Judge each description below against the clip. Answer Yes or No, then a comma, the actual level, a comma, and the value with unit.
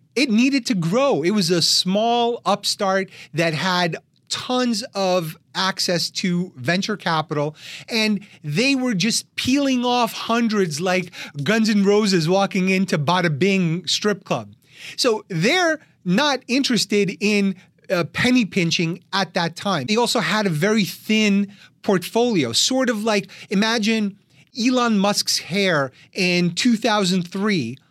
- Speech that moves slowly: Yes, slow, 130 wpm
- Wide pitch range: No, average, 4.1 semitones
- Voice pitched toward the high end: Yes, high, 195 Hz